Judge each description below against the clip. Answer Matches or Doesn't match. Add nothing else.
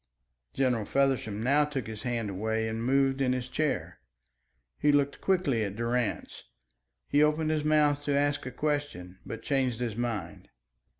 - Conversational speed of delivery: Matches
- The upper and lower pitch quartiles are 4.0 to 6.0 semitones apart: Matches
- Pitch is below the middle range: Matches